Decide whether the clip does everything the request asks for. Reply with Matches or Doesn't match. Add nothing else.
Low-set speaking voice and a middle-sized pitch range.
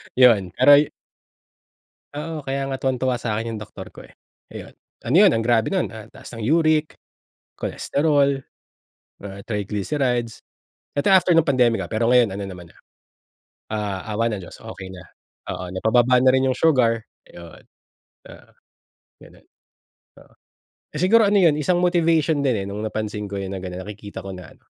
Doesn't match